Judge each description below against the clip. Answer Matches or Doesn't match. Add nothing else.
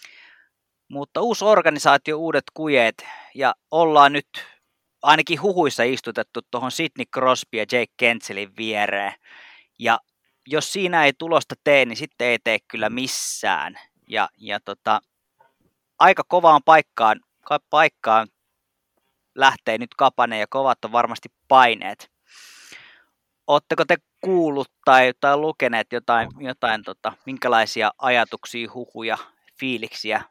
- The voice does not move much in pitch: Doesn't match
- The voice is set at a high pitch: Doesn't match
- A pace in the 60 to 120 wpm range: Matches